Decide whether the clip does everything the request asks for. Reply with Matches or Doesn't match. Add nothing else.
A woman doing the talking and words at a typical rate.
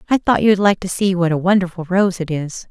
Doesn't match